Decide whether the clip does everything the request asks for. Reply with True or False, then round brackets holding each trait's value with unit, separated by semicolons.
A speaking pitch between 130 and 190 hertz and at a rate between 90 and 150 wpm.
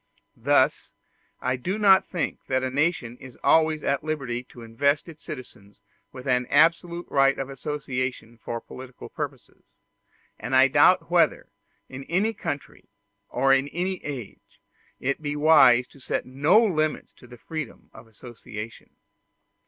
True (135 Hz; 145 wpm)